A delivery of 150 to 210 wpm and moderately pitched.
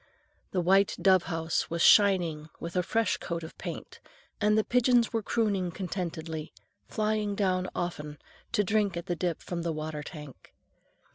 Yes: average, 160 wpm; medium, 180 Hz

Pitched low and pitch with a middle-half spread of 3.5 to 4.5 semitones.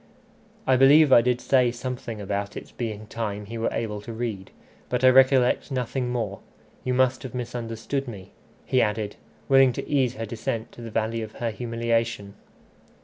No: low, 115 Hz; narrow, 2.5 semitones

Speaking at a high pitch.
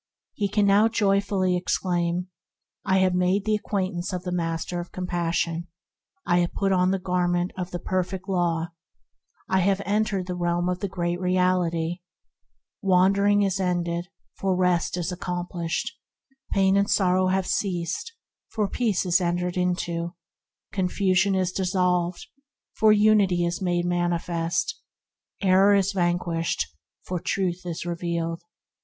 No: medium, 180 Hz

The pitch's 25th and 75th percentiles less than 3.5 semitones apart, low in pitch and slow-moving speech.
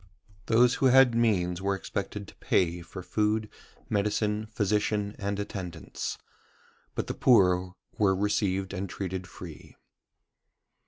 Yes: narrow, 2.5 semitones; low, 100 Hz; slow, 120 wpm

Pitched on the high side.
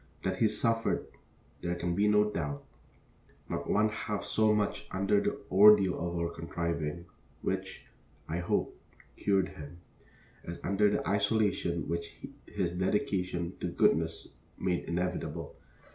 No: very low, 90 Hz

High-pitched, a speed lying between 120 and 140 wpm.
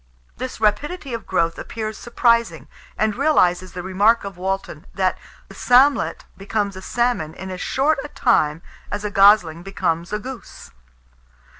No: high, 205 Hz; average, 150 wpm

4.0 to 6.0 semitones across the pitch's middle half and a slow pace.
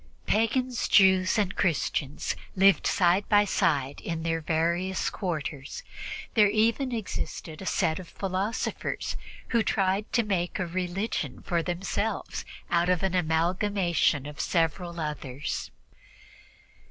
No: average, 3.6 semitones; slow, 120 wpm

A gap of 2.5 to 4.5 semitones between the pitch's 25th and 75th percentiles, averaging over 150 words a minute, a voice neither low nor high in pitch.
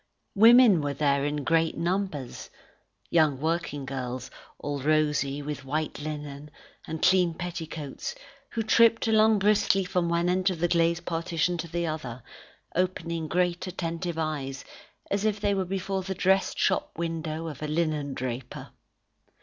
No: average, 3.7 semitones; average, 145 wpm; medium, 165 Hz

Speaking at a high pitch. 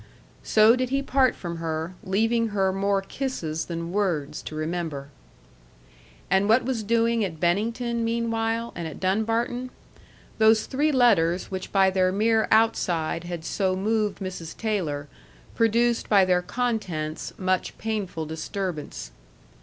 Yes: high, 200 Hz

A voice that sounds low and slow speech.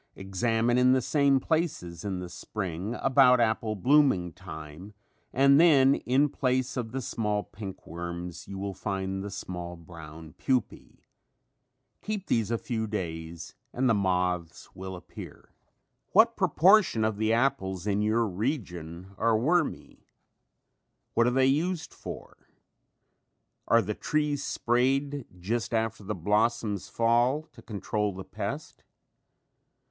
Yes: low, 110 Hz; slow, 130 wpm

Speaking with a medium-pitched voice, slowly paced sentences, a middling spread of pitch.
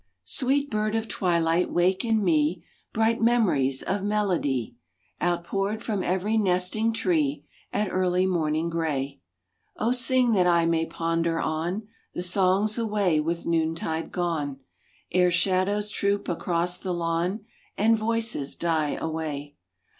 Yes: medium, 180 Hz; slow, 130 wpm; average, 4.3 semitones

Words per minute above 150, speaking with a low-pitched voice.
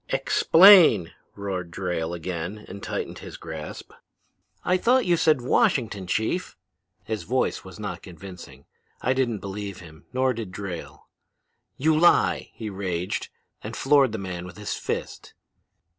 No: slow, 135 wpm; low, 100 Hz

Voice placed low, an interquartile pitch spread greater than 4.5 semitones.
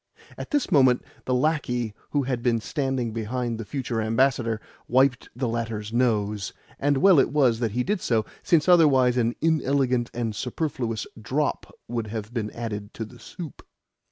No: low, 125 Hz; average, 3.3 semitones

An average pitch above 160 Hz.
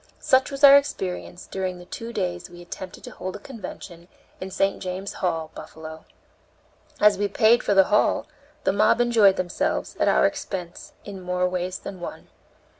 Yes: high, 190 Hz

